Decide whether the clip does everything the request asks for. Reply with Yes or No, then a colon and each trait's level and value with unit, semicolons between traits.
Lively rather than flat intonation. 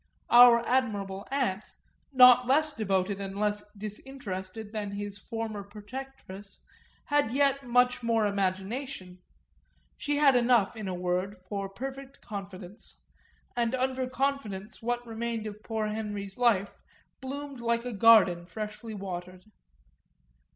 No: average, 4.0 semitones